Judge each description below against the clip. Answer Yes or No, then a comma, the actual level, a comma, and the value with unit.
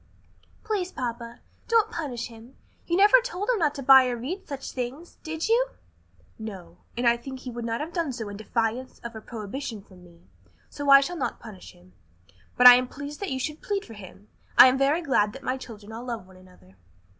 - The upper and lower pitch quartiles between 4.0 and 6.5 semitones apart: Yes, average, 5.3 semitones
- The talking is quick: Yes, fast, 215 wpm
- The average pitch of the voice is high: Yes, very high, 255 Hz